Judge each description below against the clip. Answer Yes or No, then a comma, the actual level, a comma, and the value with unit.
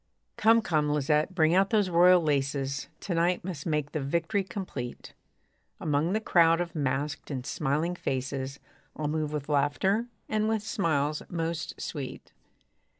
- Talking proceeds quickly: No, average, 150 wpm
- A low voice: No, medium, 155 Hz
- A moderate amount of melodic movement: Yes, average, 3.9 semitones